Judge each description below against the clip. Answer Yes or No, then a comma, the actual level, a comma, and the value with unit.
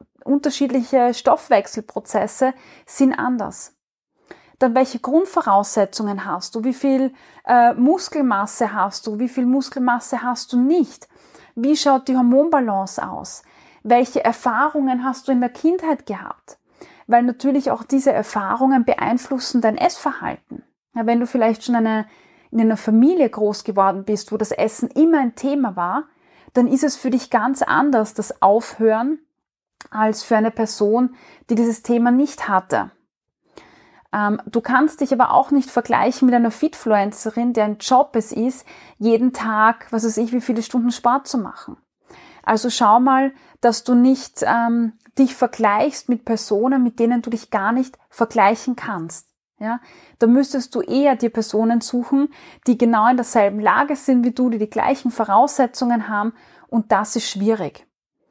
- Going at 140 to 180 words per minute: Yes, average, 150 wpm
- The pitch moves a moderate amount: Yes, average, 3.0 semitones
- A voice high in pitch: Yes, high, 245 Hz